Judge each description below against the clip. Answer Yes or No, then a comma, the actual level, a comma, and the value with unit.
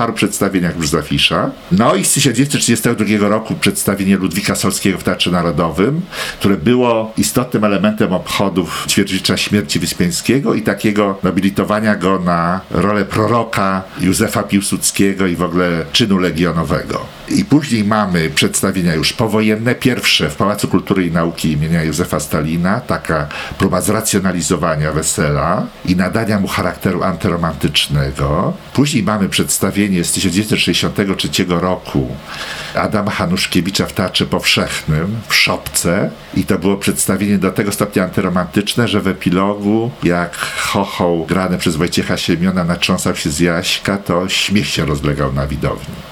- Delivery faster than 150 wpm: No, average, 130 wpm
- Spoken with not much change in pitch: No, average, 3.3 semitones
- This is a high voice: No, very low, 95 Hz